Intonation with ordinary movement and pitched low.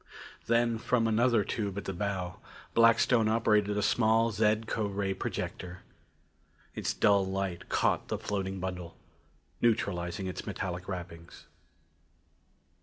Yes: average, 3.3 semitones; low, 100 Hz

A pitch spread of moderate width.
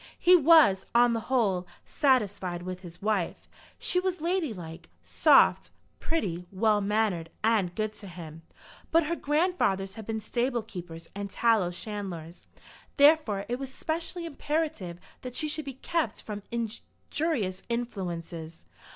No: wide, 7.7 semitones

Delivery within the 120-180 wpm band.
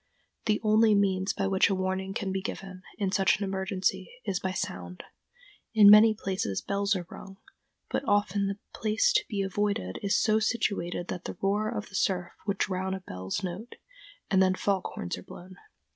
No: average, 190 wpm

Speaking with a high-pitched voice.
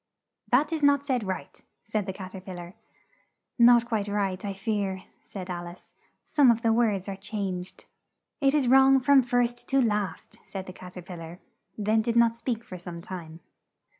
Yes: high, 210 Hz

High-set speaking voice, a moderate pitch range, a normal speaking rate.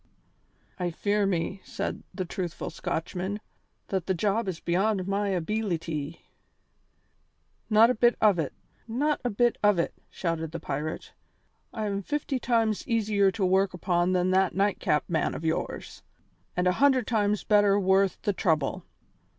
Yes: high, 195 Hz; average, 3.4 semitones; average, 150 wpm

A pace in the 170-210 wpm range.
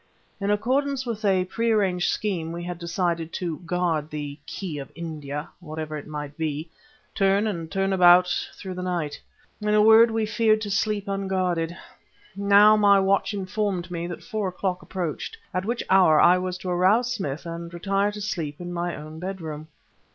Yes: average, 180 wpm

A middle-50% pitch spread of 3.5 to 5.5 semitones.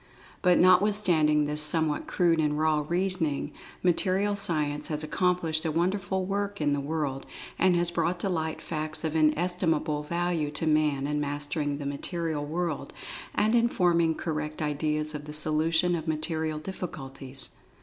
No: average, 2.9 semitones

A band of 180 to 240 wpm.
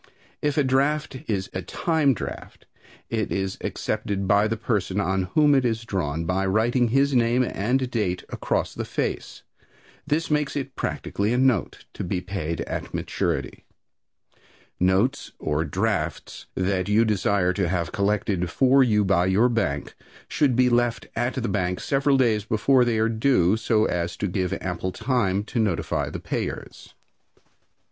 No: average, 160 wpm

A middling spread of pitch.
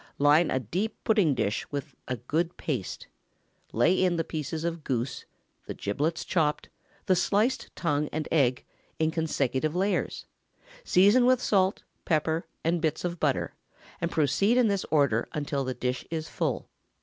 Yes: average, 3.9 semitones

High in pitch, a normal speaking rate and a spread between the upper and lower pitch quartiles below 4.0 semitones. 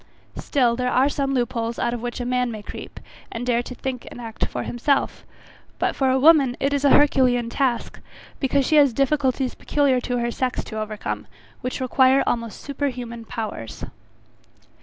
Yes: very high, 250 Hz; average, 185 wpm; narrow, 2.4 semitones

